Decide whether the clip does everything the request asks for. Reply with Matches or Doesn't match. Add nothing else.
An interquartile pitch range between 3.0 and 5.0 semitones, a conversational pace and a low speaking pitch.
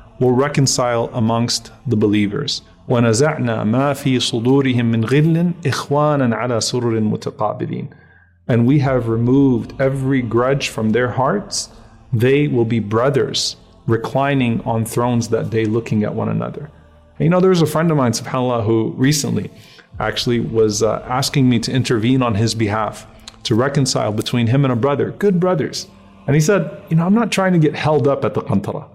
Matches